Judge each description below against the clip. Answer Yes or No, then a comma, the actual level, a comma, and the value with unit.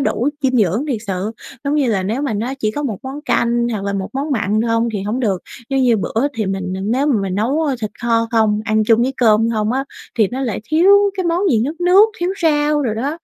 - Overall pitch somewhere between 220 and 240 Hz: Yes, high, 235 Hz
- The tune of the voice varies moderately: Yes, average, 4.7 semitones